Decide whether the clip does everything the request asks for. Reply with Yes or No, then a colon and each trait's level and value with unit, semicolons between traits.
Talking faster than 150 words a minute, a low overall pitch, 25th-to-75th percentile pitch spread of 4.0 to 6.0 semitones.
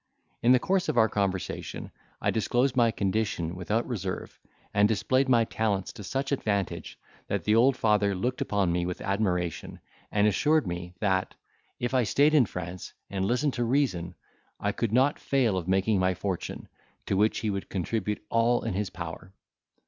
Yes: average, 175 wpm; low, 105 Hz; average, 4.5 semitones